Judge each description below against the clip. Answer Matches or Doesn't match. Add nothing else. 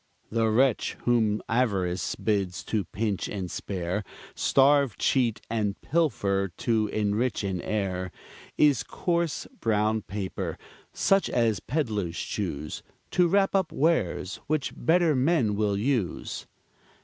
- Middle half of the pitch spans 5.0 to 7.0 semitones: Matches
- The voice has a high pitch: Doesn't match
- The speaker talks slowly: Matches